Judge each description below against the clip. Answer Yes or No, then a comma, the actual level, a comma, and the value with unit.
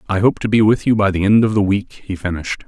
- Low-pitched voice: Yes, low, 100 Hz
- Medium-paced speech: No, fast, 315 wpm